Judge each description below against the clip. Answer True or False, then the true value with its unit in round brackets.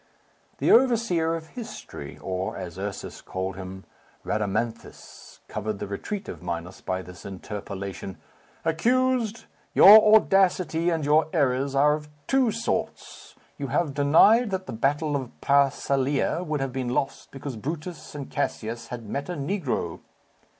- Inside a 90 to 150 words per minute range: True (140 wpm)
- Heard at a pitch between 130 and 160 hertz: True (140 Hz)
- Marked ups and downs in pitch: True (8.6 semitones)